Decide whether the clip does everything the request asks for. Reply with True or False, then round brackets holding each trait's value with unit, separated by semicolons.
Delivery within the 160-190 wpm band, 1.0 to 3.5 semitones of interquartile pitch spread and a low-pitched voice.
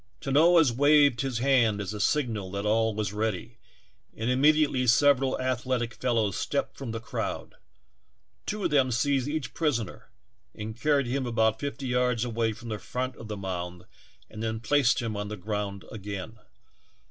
False (165 wpm; 4.0 semitones; 120 Hz)